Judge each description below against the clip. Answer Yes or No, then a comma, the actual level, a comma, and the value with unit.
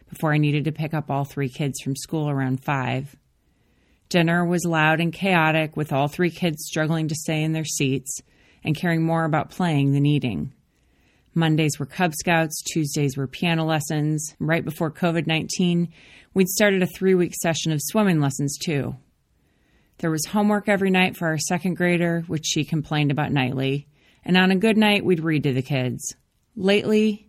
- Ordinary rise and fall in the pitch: Yes, average, 3.4 semitones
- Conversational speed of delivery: Yes, average, 180 wpm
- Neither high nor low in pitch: Yes, medium, 160 Hz